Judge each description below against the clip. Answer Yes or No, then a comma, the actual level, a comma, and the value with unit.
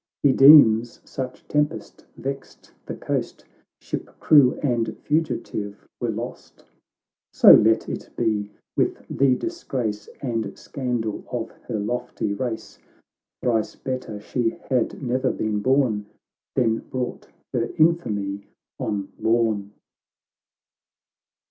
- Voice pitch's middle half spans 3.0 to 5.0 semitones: Yes, average, 3.5 semitones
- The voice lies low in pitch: Yes, low, 120 Hz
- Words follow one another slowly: Yes, slow, 115 wpm